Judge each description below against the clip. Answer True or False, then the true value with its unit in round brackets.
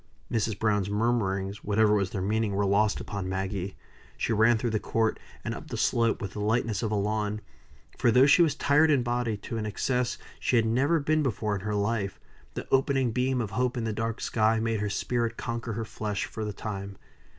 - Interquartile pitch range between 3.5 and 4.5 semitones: False (2.7 semitones)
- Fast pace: True (215 wpm)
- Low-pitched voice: True (110 Hz)